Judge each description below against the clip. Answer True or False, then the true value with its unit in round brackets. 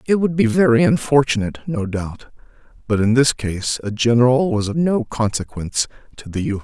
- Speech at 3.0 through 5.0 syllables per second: False (5.3 syllables/s)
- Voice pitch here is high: False (120 Hz)